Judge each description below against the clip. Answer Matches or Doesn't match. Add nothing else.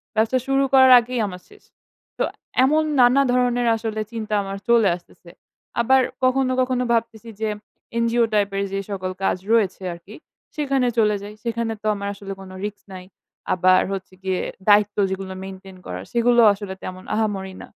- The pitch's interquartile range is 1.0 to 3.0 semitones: Doesn't match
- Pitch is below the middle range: Doesn't match